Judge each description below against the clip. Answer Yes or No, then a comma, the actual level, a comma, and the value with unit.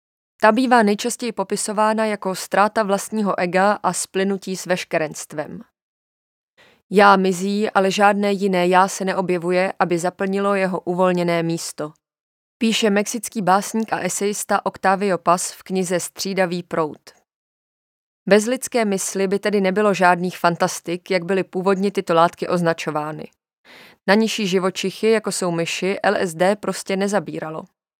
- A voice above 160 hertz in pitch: Yes, high, 190 Hz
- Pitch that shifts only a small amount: Yes, narrow, 2.3 semitones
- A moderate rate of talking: Yes, average, 125 wpm